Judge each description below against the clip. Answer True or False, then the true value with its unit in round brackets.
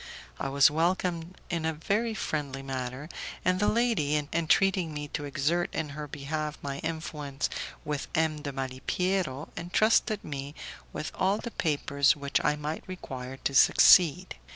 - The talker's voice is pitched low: False (150 Hz)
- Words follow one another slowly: False (150 wpm)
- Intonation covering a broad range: False (4.0 semitones)